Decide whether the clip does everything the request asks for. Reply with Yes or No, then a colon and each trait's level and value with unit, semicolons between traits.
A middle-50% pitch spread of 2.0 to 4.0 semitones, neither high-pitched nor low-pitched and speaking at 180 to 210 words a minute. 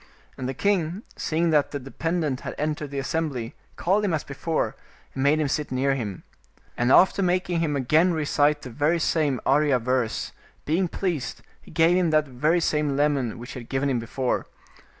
Yes: average, 3.6 semitones; medium, 150 Hz; average, 190 wpm